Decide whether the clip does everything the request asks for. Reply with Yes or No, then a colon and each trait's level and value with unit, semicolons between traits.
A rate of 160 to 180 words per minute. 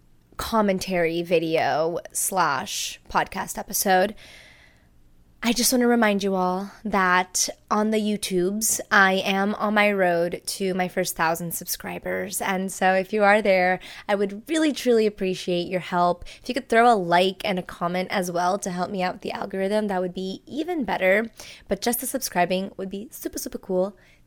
Yes: average, 175 wpm